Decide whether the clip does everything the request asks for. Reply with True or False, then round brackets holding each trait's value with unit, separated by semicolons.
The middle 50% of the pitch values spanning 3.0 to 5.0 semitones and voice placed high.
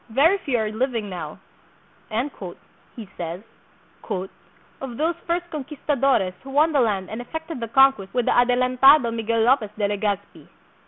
True (4.5 semitones; 245 Hz)